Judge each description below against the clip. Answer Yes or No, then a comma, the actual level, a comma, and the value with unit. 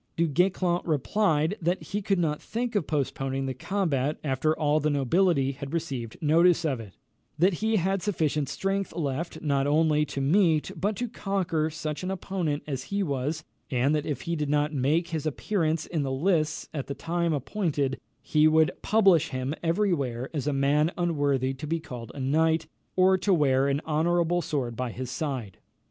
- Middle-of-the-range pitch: Yes, medium, 155 Hz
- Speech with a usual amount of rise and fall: Yes, average, 4.0 semitones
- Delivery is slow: No, average, 185 wpm